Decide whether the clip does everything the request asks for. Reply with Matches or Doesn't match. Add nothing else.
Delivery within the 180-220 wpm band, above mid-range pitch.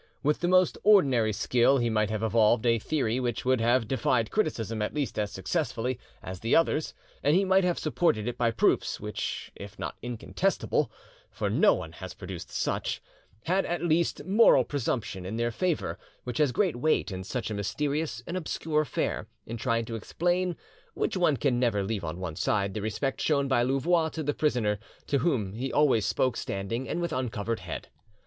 Doesn't match